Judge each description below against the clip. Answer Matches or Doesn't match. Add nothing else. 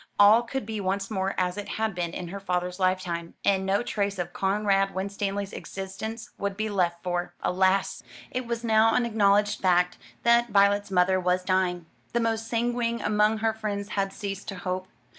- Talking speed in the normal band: Matches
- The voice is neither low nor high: Doesn't match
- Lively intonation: Doesn't match